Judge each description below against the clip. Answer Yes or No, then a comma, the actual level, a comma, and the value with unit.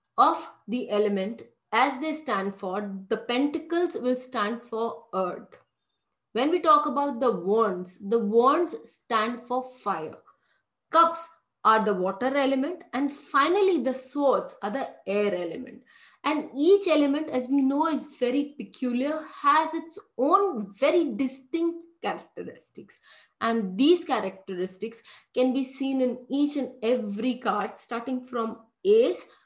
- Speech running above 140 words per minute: No, slow, 135 wpm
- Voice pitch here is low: No, very high, 255 Hz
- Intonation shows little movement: No, average, 5.1 semitones